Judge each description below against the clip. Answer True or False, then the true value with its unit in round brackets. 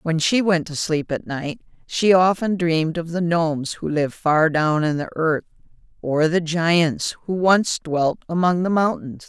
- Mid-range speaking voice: True (165 Hz)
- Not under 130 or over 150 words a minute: False (190 wpm)